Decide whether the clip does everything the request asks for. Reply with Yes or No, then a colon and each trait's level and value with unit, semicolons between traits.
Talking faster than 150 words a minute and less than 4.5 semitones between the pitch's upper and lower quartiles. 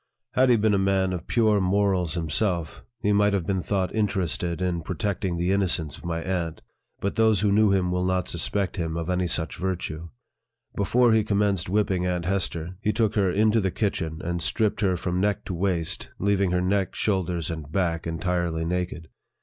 Yes: average, 190 wpm; average, 2.9 semitones